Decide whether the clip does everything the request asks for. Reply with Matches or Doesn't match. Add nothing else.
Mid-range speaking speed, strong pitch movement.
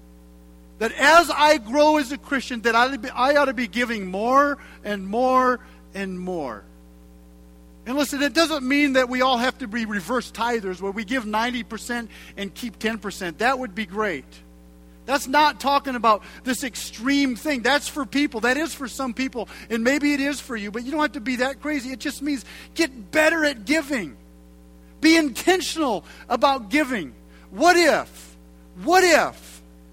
Matches